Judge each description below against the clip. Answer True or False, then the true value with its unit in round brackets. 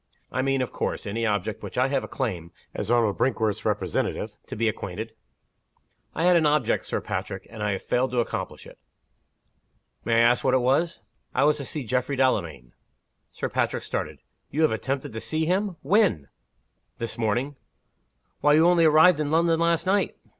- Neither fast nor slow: True (190 wpm)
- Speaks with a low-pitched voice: True (130 Hz)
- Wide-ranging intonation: True (5.8 semitones)